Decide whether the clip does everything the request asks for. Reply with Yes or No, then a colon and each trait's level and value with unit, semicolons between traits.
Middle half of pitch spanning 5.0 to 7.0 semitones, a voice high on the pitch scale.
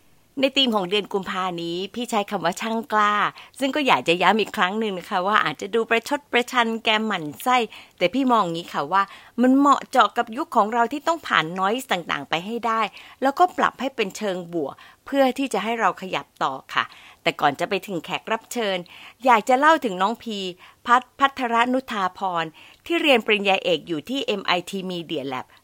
Yes: average, 5.3 semitones; high, 220 Hz